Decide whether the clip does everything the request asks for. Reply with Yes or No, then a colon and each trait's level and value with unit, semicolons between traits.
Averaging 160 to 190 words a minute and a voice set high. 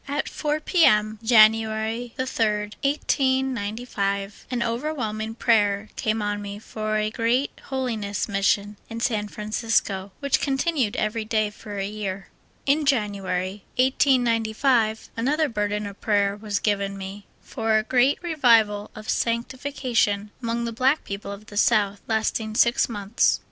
No: average, 140 wpm; high, 220 Hz